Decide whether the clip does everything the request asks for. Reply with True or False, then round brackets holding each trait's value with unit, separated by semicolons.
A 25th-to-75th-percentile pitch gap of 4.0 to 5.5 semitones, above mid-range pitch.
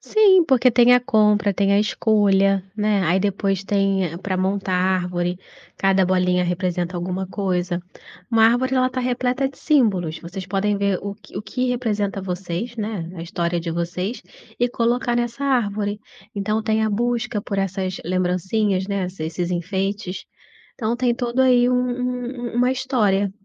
True (4.5 semitones; 200 Hz)